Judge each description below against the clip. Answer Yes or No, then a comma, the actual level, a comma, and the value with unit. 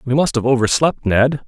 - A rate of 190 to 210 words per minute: Yes, fast, 205 wpm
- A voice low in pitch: Yes, low, 130 Hz